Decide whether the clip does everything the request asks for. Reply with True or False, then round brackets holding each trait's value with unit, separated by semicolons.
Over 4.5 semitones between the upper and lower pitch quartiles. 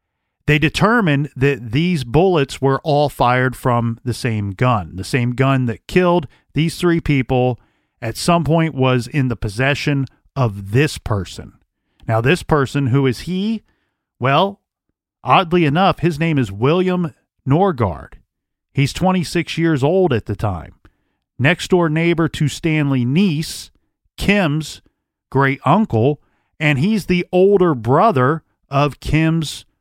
True (4.9 semitones)